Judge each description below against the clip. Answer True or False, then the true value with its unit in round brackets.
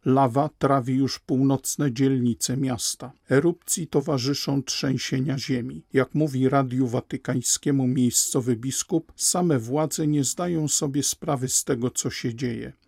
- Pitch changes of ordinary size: False (2.1 semitones)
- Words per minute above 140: False (125 wpm)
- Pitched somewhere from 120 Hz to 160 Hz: True (135 Hz)